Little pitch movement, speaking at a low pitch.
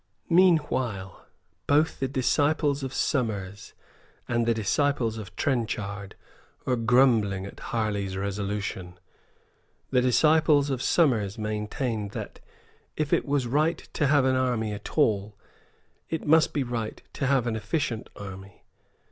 No: wide, 5.5 semitones; low, 120 Hz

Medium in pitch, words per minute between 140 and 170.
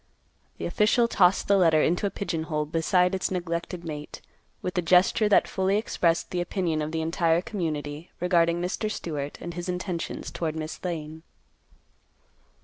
Yes: medium, 175 Hz; average, 160 wpm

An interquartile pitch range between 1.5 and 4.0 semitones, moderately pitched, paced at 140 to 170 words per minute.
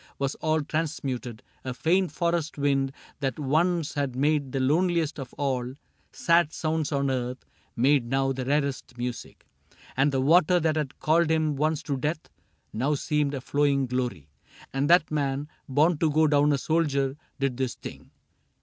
Yes: average, 2.8 semitones; medium, 145 Hz; average, 165 wpm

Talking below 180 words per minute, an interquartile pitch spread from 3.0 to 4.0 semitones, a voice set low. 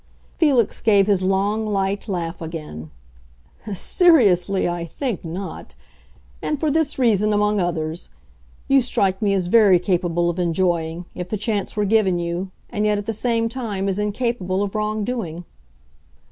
No: average, 155 wpm; average, 3.7 semitones; high, 200 Hz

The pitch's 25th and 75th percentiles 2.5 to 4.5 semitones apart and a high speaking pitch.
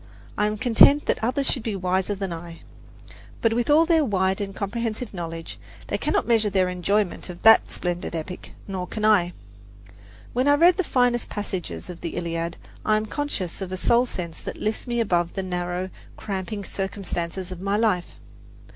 Yes: average, 4.1 semitones; high, 195 Hz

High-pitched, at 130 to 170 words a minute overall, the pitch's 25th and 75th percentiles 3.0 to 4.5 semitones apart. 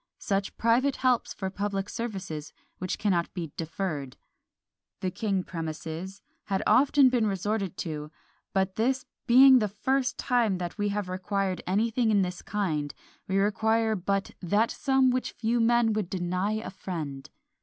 Yes: high, 200 Hz; average, 150 wpm; average, 3.9 semitones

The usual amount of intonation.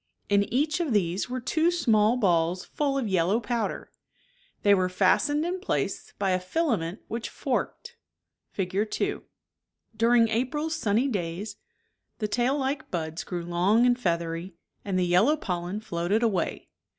No: wide, 5.8 semitones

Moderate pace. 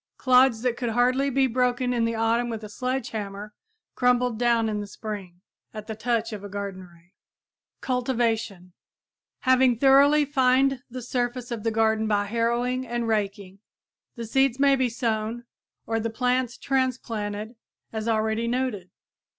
Yes: average, 155 wpm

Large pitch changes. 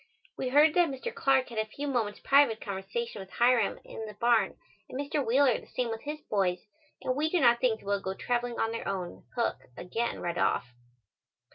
No: average, 4.7 semitones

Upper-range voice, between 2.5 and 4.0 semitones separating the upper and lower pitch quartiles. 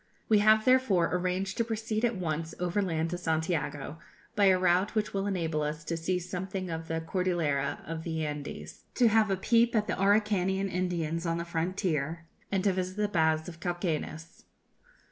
No: medium, 180 Hz; average, 3.4 semitones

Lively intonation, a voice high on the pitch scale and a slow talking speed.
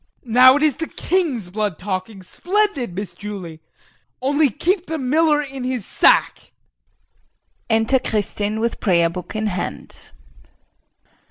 Yes: wide, 6.6 semitones; high, 230 Hz; slow, 125 wpm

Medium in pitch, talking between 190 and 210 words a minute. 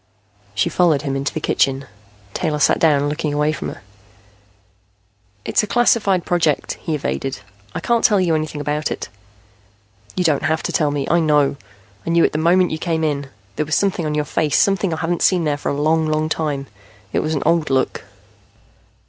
Yes: medium, 155 Hz; average, 200 wpm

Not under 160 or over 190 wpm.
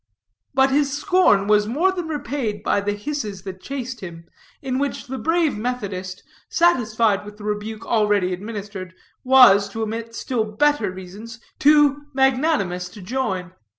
No: average, 150 wpm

